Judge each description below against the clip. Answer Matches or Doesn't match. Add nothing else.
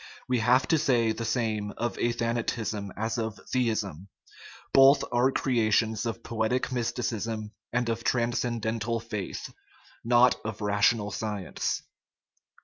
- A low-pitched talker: Matches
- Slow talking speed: Matches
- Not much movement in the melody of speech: Matches